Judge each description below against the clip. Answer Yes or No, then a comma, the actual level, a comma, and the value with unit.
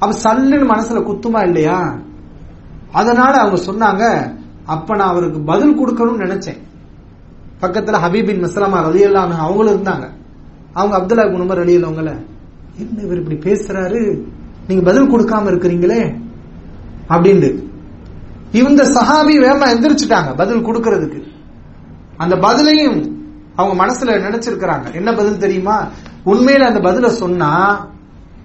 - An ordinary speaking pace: No, slow, 110 wpm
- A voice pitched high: Yes, high, 195 Hz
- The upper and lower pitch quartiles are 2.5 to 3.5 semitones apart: No, average, 4.7 semitones